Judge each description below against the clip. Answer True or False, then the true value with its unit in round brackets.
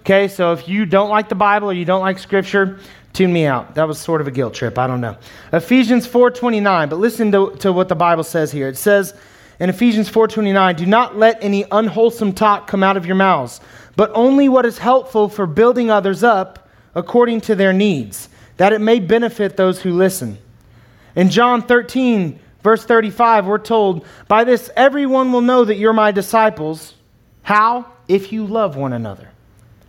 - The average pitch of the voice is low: False (200 Hz)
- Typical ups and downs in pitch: True (4.6 semitones)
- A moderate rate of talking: True (190 wpm)